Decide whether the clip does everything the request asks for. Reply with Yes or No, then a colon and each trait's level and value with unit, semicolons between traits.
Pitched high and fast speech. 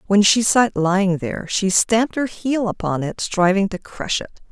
Yes: high, 200 Hz; fast, 215 wpm